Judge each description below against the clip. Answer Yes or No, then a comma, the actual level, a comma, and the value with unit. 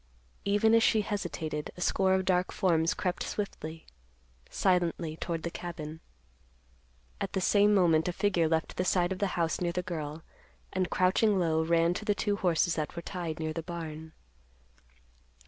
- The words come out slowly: No, average, 170 wpm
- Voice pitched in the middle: Yes, medium, 175 Hz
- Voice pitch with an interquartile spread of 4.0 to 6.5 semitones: No, average, 2.8 semitones